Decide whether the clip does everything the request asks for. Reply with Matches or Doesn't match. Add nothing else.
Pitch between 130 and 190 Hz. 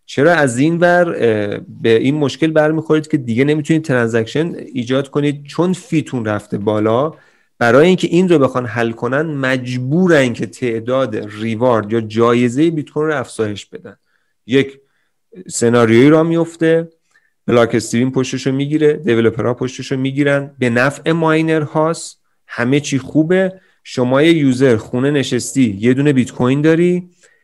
Matches